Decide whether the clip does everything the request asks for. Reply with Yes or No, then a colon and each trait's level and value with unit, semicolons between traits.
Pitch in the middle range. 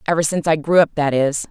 Yes: medium, 155 Hz